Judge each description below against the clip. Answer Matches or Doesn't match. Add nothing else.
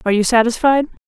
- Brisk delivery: Doesn't match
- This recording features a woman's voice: Matches